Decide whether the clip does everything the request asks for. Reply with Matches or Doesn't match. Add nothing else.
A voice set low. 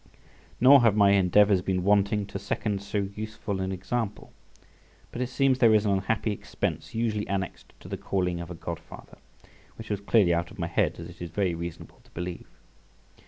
Matches